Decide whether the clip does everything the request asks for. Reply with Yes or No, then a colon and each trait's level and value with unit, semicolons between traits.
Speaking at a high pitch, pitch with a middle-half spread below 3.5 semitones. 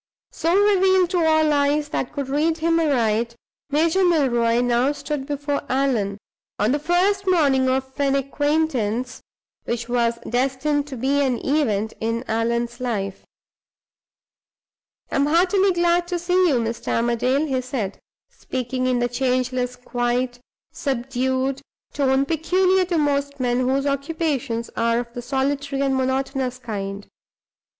No: very high, 270 Hz; average, 3.8 semitones